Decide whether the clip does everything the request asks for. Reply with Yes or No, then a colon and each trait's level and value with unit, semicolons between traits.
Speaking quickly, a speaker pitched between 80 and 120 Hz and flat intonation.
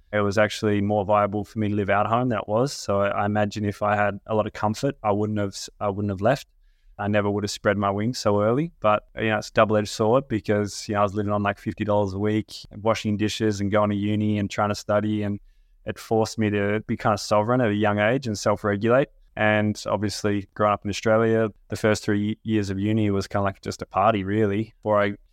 Yes: fast, 255 wpm; low, 105 Hz; narrow, 0.9 semitones